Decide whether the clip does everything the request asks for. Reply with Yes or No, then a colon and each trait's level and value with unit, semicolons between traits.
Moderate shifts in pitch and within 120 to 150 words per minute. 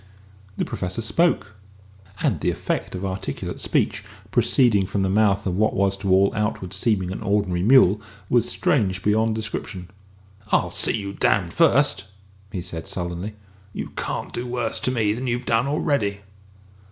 No: average, 3.3 semitones; average, 160 wpm